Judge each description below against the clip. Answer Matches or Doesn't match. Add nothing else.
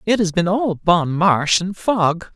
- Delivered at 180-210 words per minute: Matches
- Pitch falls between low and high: Matches